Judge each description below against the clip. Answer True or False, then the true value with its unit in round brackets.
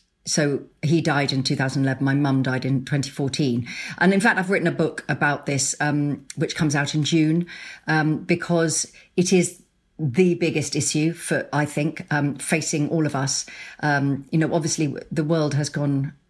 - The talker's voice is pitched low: False (150 Hz)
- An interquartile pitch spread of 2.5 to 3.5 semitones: True (2.8 semitones)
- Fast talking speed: False (175 wpm)